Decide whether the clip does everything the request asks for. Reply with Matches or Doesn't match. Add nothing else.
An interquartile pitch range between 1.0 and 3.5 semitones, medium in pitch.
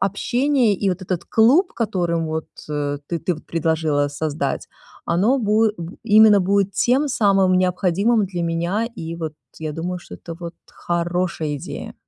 Doesn't match